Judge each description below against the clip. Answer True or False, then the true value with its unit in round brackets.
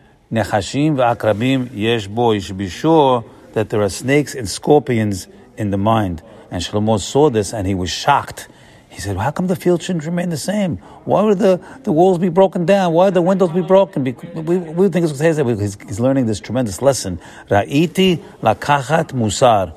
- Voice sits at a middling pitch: False (130 Hz)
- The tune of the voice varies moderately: False (8.5 semitones)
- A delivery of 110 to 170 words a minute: False (180 wpm)